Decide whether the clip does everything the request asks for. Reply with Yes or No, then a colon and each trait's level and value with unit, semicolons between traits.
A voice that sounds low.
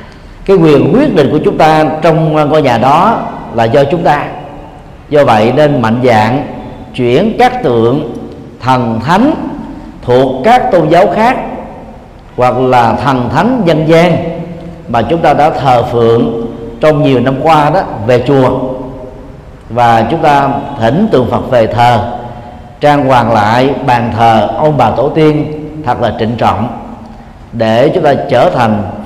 Yes: low, 130 Hz